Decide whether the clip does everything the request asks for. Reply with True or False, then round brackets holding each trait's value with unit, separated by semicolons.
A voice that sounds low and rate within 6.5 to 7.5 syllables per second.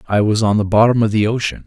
True (105 Hz; 6.7 syllables/s)